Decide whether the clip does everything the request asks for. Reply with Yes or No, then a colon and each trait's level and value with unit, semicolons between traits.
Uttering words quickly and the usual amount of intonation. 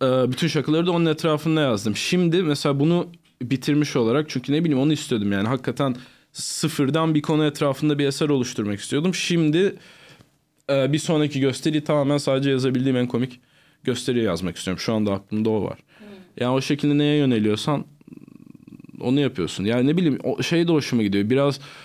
Yes: fast, 160 wpm; average, 3.6 semitones